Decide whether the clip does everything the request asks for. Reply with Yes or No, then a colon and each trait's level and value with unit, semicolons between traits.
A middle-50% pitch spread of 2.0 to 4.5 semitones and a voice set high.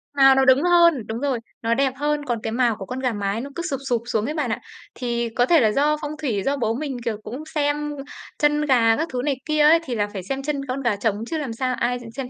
Yes: average, 4.1 semitones; very high, 260 Hz